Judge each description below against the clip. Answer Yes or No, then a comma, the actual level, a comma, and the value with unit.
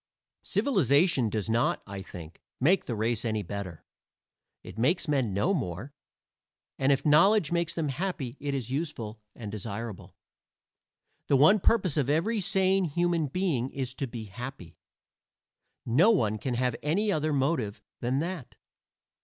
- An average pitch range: No, wide, 7.1 semitones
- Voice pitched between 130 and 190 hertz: Yes, low, 135 Hz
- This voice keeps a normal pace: Yes, average, 145 wpm